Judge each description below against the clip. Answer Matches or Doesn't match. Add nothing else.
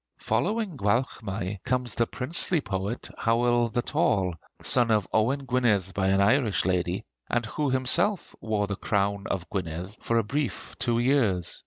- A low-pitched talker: Matches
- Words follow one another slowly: Doesn't match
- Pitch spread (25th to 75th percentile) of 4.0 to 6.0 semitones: Matches